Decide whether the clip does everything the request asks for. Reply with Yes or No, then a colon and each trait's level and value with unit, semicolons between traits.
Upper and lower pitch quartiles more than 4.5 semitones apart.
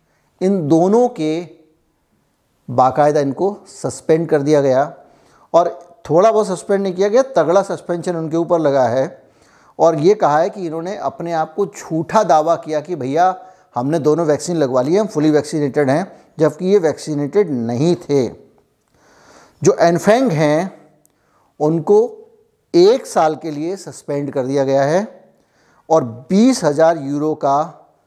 No: average, 4.1 semitones